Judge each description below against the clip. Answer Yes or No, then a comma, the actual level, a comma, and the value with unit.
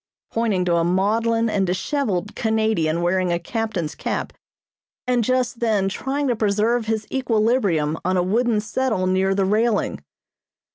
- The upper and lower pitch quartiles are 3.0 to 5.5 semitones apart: Yes, average, 3.8 semitones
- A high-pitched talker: Yes, high, 215 Hz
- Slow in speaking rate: No, average, 145 wpm